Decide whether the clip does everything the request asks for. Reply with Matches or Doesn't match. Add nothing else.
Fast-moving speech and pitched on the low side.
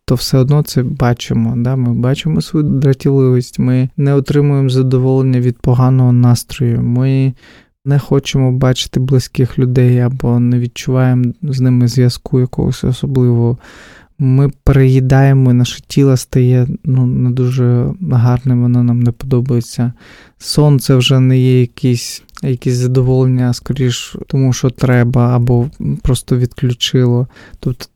Doesn't match